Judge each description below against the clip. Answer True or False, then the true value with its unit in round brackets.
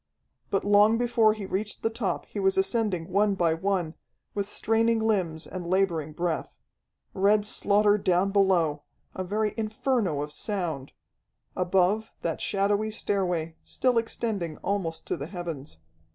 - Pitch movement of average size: True (3.8 semitones)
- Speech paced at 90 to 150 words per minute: True (140 wpm)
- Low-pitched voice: False (195 Hz)